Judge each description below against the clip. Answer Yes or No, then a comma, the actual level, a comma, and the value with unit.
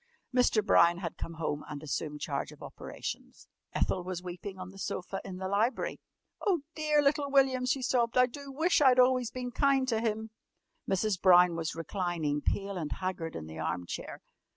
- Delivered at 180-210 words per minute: Yes, average, 185 wpm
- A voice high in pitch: Yes, high, 195 Hz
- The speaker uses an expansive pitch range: Yes, wide, 6.8 semitones